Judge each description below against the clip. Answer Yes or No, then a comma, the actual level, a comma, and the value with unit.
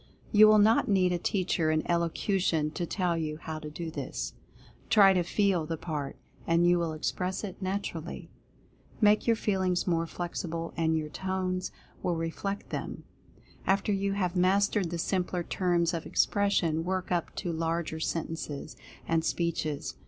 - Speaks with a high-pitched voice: No, medium, 175 Hz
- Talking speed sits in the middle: Yes, average, 160 wpm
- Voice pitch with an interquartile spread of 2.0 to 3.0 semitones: Yes, average, 2.7 semitones